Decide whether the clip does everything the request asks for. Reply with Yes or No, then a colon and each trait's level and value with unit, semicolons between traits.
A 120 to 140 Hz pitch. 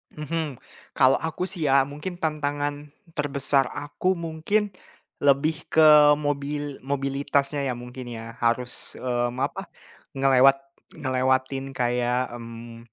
Yes: low, 135 Hz